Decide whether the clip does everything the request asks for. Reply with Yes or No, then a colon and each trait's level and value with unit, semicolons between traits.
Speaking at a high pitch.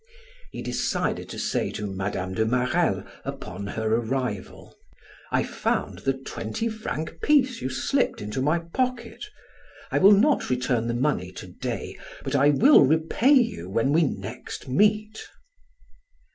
No: low, 135 Hz